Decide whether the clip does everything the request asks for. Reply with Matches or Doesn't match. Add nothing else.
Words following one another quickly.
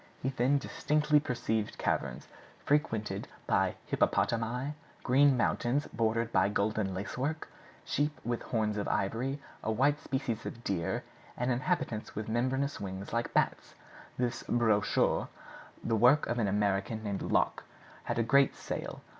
Doesn't match